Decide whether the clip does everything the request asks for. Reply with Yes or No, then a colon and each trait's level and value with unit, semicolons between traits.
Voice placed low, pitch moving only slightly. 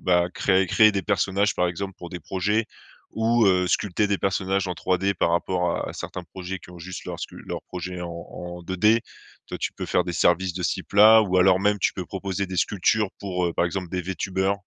Yes: very low, 95 Hz; narrow, 1.9 semitones